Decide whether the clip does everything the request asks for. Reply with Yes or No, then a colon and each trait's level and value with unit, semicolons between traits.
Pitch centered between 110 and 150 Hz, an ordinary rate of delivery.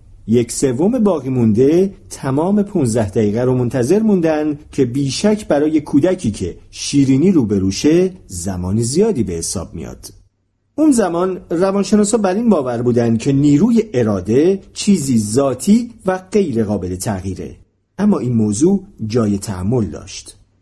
Yes: low, 125 Hz; average, 130 wpm